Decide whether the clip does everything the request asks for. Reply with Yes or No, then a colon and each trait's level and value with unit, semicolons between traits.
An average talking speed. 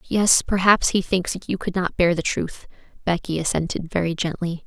Yes: average, 180 wpm